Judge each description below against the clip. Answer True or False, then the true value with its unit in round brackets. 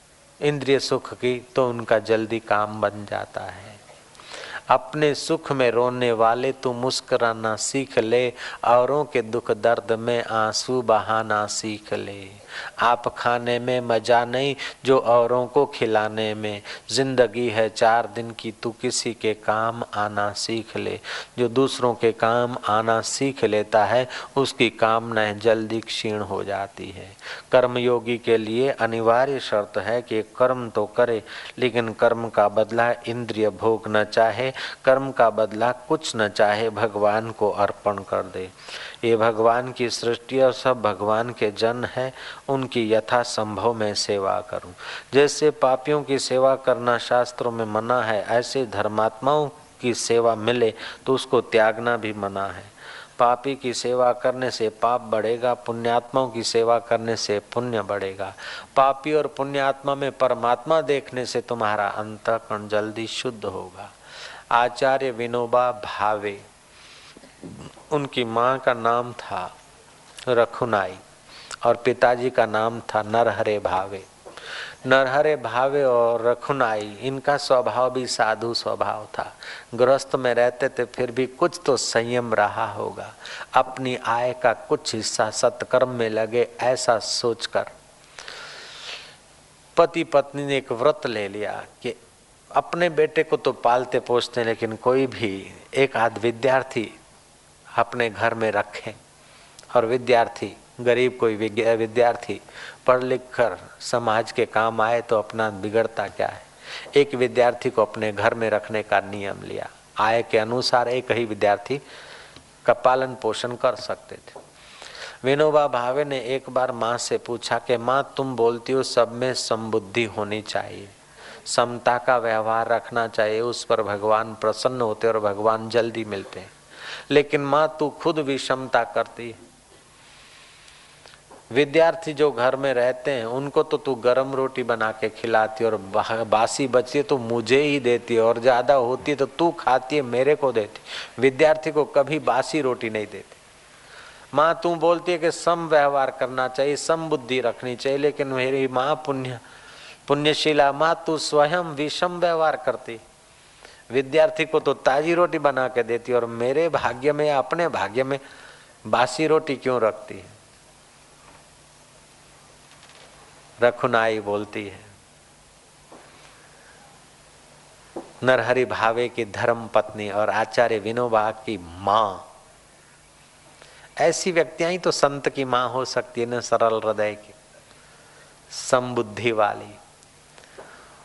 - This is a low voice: True (120 Hz)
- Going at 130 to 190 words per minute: True (140 wpm)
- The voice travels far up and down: False (3.0 semitones)